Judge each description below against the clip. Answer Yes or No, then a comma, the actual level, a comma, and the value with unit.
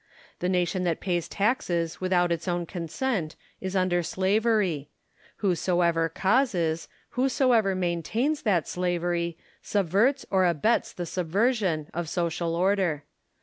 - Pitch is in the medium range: Yes, medium, 180 Hz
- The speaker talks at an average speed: No, slow, 115 wpm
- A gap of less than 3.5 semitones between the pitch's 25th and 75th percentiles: Yes, average, 3.1 semitones